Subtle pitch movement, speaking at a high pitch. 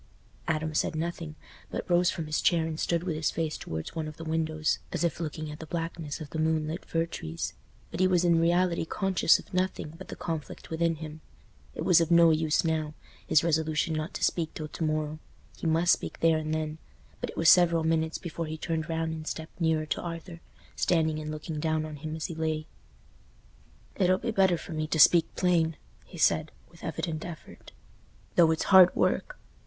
No: narrow, 1.5 semitones; medium, 160 Hz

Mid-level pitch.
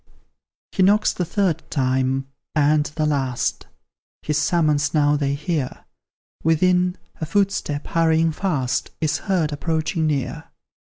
Yes: medium, 155 Hz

